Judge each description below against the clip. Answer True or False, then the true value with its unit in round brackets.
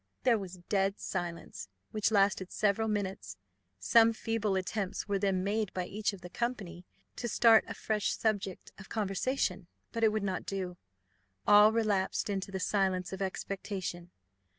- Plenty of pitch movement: False (2.5 semitones)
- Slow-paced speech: False (160 wpm)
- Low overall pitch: False (195 Hz)